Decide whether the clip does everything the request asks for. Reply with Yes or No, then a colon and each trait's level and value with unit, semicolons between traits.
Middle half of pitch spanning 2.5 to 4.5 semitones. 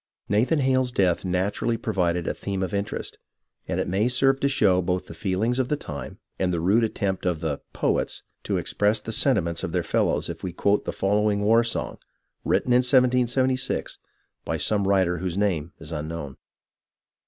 No: average, 5.1 semitones